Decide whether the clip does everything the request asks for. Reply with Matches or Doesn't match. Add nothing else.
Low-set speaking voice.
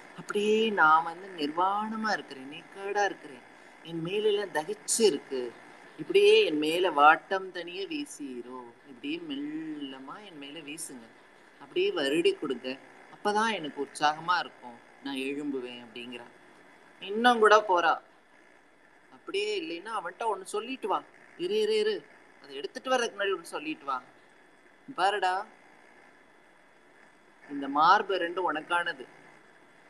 Doesn't match